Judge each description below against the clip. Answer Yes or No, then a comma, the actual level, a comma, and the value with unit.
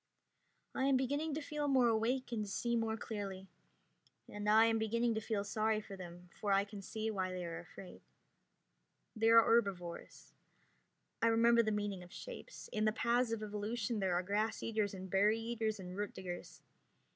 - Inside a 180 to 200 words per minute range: Yes, average, 185 wpm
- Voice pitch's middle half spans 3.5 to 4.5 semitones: No, average, 2.7 semitones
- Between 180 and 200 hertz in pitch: No, high, 215 Hz